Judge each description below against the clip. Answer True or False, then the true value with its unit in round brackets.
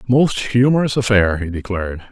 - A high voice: False (110 Hz)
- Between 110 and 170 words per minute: True (140 wpm)